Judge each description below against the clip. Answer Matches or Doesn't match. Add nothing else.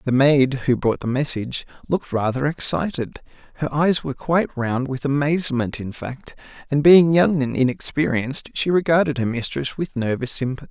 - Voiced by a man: Matches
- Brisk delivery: Doesn't match